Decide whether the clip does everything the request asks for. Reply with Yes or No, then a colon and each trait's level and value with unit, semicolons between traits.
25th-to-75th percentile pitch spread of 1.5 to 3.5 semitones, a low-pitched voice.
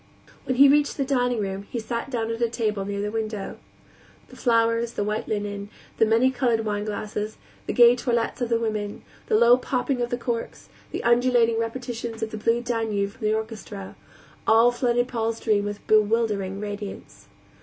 No: narrow, 2.4 semitones; high, 225 Hz